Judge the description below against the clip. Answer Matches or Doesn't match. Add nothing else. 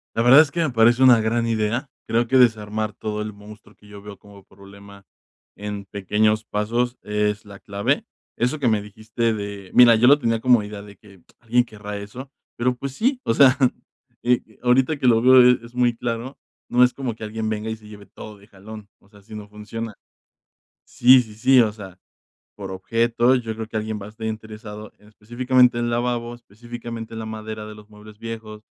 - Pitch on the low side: Matches